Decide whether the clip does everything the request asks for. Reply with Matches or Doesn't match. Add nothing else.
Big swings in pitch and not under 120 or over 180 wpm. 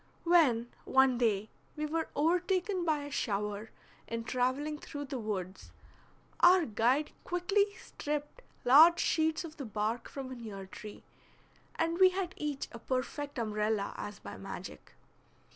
Matches